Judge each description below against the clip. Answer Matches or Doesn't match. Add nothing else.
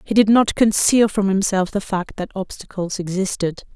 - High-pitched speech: Matches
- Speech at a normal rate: Matches